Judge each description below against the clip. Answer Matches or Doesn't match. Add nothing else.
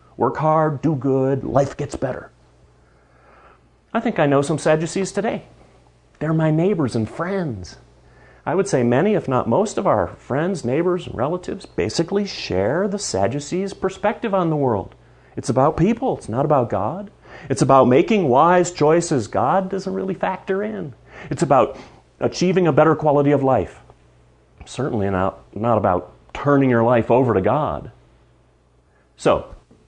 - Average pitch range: Doesn't match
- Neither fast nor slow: Matches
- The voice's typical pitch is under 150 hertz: Matches